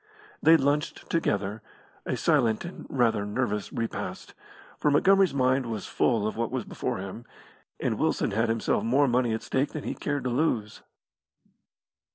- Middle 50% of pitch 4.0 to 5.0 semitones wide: Yes, average, 4.3 semitones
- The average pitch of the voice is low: Yes, low, 120 Hz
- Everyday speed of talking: Yes, average, 160 wpm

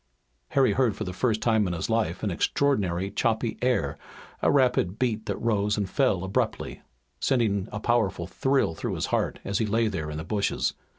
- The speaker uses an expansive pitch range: No, average, 4.1 semitones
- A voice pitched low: Yes, low, 105 Hz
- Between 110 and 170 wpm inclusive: No, average, 190 wpm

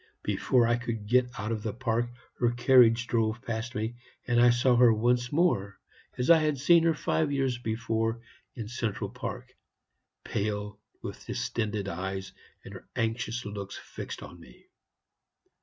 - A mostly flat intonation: Yes, narrow, 2.3 semitones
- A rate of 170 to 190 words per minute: No, average, 155 wpm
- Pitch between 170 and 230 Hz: No, low, 115 Hz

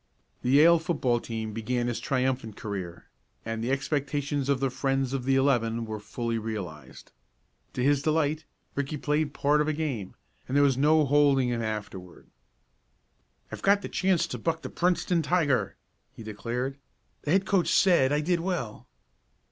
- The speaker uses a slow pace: No, average, 165 wpm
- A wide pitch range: No, average, 4.7 semitones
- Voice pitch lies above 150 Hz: No, low, 135 Hz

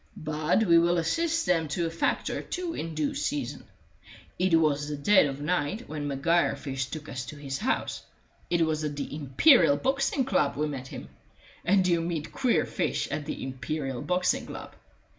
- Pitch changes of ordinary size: Yes, average, 3.9 semitones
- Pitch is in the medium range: Yes, medium, 155 Hz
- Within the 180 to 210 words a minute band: Yes, average, 185 wpm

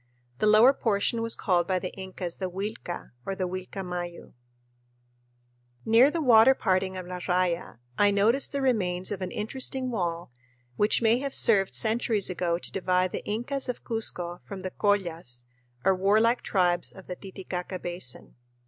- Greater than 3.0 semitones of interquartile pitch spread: Yes, average, 3.7 semitones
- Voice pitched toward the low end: No, high, 190 Hz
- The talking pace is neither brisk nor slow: Yes, average, 160 wpm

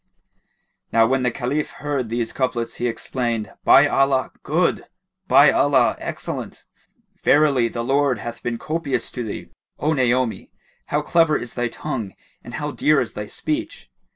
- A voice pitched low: Yes, low, 130 Hz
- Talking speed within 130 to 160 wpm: Yes, average, 155 wpm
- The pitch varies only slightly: No, average, 3.8 semitones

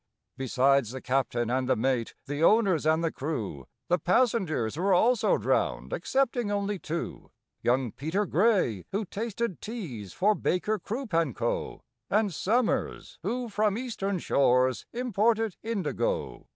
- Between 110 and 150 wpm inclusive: Yes, average, 140 wpm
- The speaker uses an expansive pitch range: Yes, wide, 8.7 semitones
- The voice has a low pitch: No, medium, 185 Hz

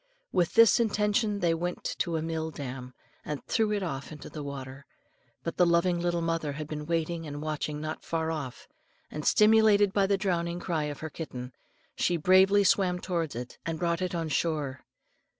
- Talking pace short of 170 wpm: No, average, 185 wpm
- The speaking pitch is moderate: Yes, medium, 165 Hz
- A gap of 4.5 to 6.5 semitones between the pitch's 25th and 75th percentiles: No, average, 3.4 semitones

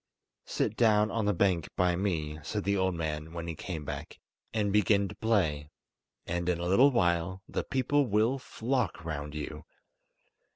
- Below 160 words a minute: No, average, 170 wpm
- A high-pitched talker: No, very low, 95 Hz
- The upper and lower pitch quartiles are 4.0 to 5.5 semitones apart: Yes, average, 4.5 semitones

